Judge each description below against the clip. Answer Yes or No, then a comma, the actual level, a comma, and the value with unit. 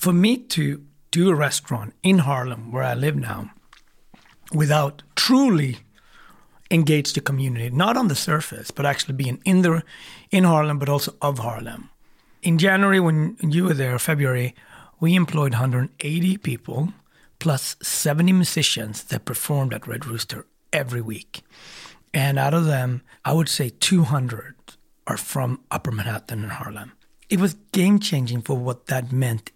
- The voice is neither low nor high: Yes, medium, 145 Hz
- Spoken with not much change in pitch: No, average, 4.9 semitones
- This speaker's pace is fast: No, average, 150 wpm